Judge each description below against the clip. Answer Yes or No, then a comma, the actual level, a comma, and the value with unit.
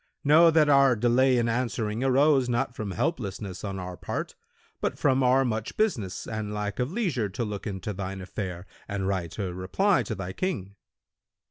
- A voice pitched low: Yes, low, 110 Hz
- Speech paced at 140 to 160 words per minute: No, average, 175 wpm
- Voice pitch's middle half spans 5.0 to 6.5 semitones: Yes, wide, 5.4 semitones